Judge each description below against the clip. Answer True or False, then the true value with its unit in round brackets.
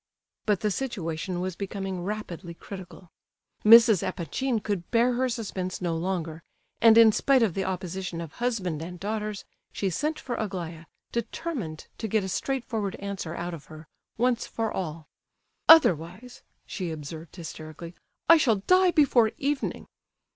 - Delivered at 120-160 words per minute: True (145 wpm)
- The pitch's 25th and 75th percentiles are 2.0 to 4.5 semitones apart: False (5.2 semitones)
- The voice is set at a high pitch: True (195 Hz)